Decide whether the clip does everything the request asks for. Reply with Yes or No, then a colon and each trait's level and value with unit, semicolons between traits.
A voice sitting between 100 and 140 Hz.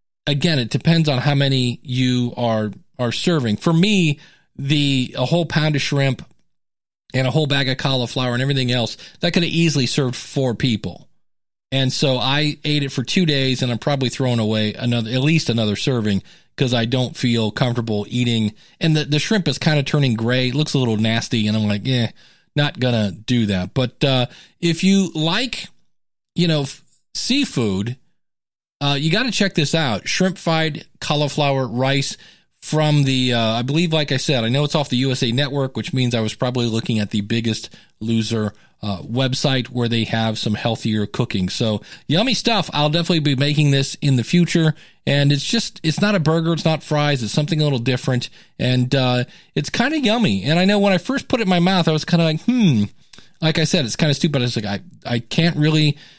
Yes: low, 135 Hz